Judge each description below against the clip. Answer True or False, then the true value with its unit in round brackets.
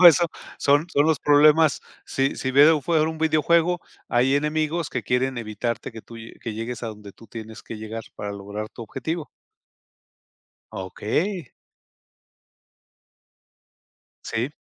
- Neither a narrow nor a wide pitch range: False (5.8 semitones)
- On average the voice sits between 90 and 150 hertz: True (135 Hz)